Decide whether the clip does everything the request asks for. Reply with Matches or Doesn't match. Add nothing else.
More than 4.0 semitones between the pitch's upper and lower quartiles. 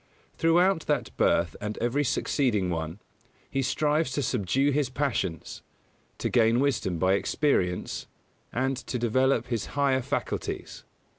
Matches